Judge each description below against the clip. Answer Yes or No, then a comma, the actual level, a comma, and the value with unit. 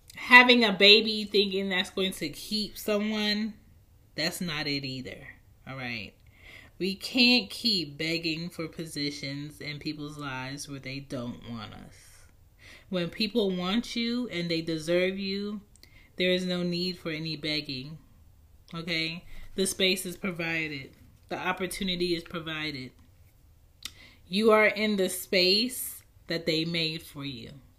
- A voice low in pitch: No, medium, 165 Hz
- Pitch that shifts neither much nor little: No, wide, 6.1 semitones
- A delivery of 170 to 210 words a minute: No, slow, 135 wpm